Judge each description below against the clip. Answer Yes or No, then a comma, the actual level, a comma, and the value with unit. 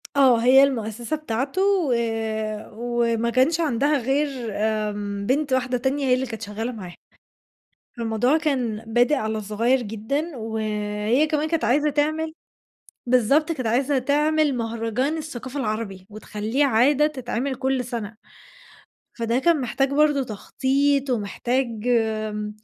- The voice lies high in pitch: Yes, very high, 250 Hz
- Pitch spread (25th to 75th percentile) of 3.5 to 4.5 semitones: Yes, average, 4.2 semitones